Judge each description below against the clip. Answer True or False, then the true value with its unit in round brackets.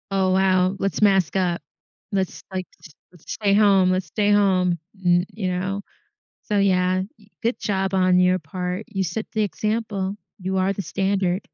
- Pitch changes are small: True (1.5 semitones)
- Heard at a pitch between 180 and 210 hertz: True (190 Hz)